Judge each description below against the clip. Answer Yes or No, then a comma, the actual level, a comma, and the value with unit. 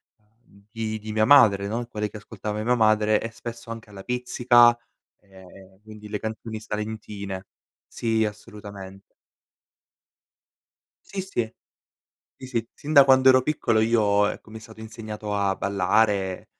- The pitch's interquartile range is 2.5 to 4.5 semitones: No, narrow, 2.0 semitones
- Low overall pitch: Yes, low, 110 Hz